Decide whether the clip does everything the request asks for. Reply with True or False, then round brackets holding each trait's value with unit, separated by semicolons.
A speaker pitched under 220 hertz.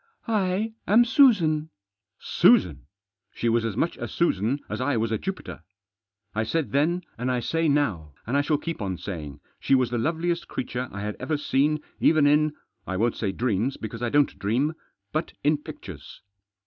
True (135 Hz)